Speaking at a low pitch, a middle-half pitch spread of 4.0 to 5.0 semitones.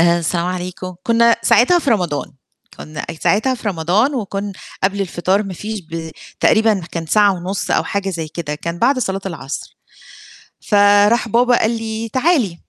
No: high, 200 Hz; average, 4.6 semitones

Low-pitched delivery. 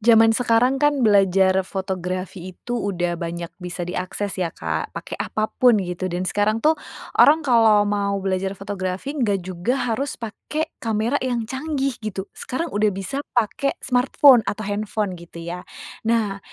No: high, 205 Hz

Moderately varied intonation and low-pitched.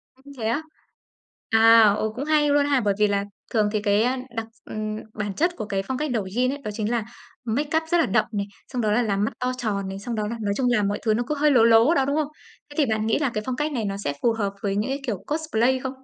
No: average, 4.5 semitones; high, 230 Hz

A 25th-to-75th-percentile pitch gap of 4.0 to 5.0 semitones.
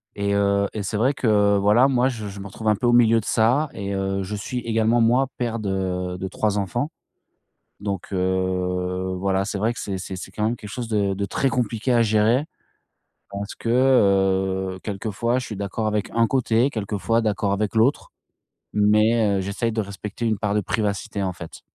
No: average, 2.8 semitones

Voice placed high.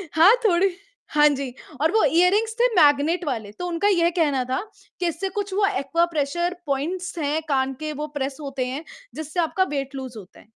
Yes: very high, 310 Hz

